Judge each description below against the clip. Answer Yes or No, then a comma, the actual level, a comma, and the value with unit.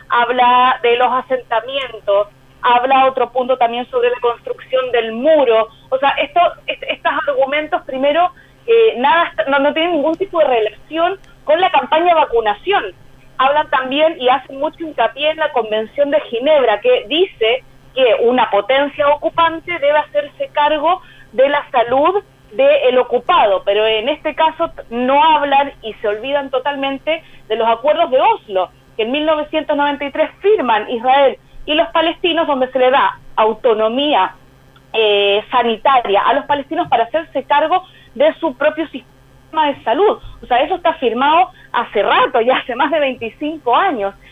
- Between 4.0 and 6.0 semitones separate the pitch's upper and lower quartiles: Yes, average, 4.5 semitones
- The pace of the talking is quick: No, average, 155 wpm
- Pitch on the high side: Yes, very high, 285 Hz